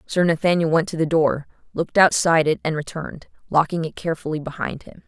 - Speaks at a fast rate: No, average, 190 wpm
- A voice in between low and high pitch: Yes, medium, 160 Hz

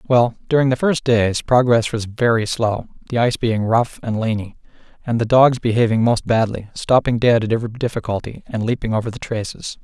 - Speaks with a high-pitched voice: No, low, 115 Hz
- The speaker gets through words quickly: No, average, 190 wpm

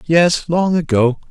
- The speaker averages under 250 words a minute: Yes, average, 140 wpm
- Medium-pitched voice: Yes, medium, 160 Hz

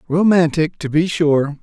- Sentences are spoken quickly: No, average, 145 wpm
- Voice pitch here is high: No, medium, 160 Hz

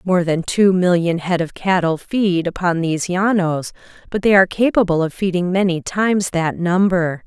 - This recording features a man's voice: No, female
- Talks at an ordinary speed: Yes, average, 175 wpm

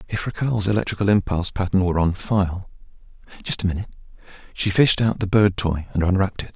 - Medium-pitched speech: No, very low, 95 Hz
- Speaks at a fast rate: No, average, 175 wpm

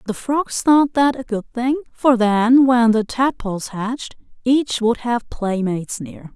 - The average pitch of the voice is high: Yes, high, 240 Hz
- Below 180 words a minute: Yes, average, 170 wpm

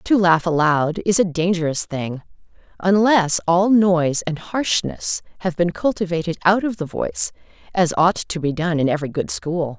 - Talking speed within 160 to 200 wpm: Yes, average, 170 wpm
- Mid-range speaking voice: Yes, medium, 165 Hz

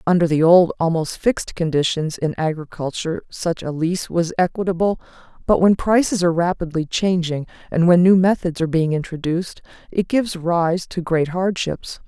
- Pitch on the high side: No, medium, 170 Hz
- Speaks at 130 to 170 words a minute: Yes, average, 160 wpm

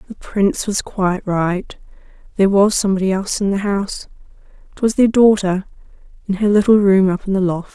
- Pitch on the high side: Yes, high, 195 Hz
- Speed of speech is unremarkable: Yes, average, 180 wpm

